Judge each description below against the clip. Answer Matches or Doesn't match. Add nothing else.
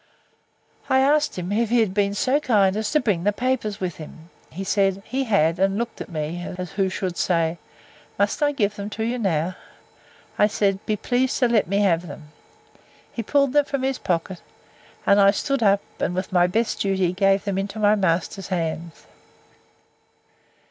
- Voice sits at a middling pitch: Doesn't match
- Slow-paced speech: Doesn't match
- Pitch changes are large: Doesn't match